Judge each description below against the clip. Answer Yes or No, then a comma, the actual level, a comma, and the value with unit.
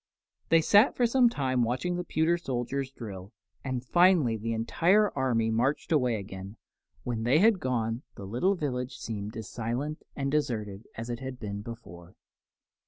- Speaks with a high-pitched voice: No, low, 125 Hz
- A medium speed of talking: Yes, average, 165 wpm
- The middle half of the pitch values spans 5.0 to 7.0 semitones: Yes, average, 5.3 semitones